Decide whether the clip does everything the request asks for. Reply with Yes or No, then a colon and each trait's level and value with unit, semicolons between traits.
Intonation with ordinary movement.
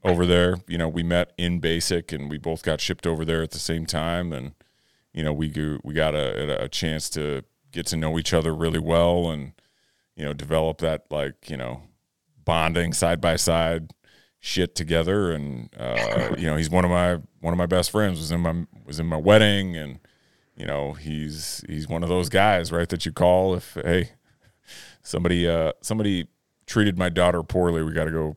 No: narrow, 2.0 semitones